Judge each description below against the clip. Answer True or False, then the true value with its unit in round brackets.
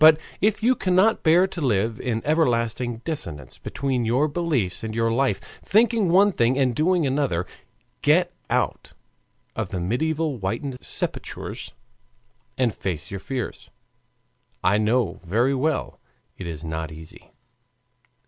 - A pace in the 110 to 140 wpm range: True (135 wpm)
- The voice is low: True (125 Hz)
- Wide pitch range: True (6.9 semitones)